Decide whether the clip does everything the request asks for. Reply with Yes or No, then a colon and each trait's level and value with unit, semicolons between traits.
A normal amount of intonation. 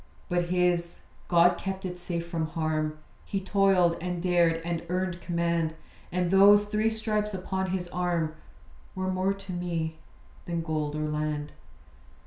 No: narrow, 2.2 semitones